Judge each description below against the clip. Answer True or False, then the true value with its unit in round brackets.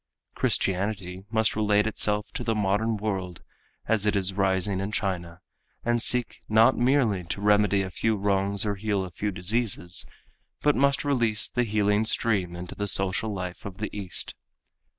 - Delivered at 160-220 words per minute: True (165 wpm)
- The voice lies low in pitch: True (105 Hz)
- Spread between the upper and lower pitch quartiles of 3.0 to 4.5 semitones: False (2.5 semitones)